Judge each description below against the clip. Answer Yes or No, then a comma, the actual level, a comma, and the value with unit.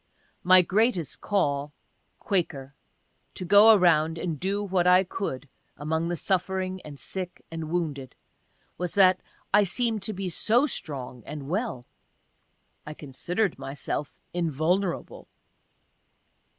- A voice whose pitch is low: No, medium, 175 Hz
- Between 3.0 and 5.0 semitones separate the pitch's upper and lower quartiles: Yes, average, 4.1 semitones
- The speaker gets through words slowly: Yes, slow, 120 wpm